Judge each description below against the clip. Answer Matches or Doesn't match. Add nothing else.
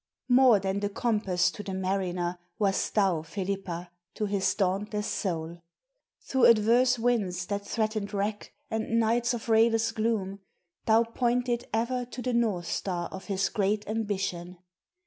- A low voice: Doesn't match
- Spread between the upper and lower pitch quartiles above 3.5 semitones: Doesn't match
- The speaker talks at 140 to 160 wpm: Matches